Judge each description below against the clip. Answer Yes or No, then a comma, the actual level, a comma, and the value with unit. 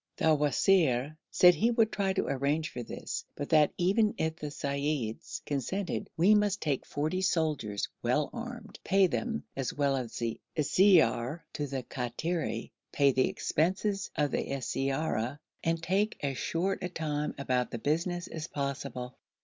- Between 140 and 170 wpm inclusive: Yes, average, 155 wpm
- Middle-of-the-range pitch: Yes, medium, 150 Hz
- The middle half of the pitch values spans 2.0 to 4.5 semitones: No, average, 4.9 semitones